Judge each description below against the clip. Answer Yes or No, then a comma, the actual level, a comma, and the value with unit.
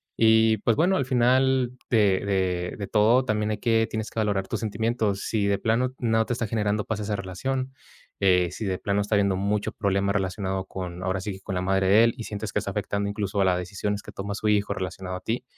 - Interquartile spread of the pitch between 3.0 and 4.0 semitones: No, narrow, 2.6 semitones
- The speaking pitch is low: Yes, low, 105 Hz